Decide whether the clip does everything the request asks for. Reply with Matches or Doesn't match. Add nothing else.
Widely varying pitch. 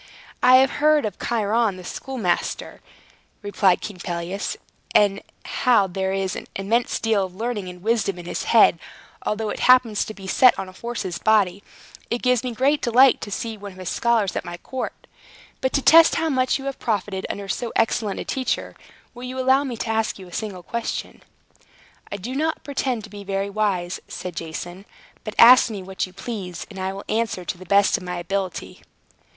Doesn't match